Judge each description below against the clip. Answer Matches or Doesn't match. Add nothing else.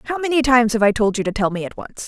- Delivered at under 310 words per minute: Doesn't match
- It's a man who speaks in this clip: Doesn't match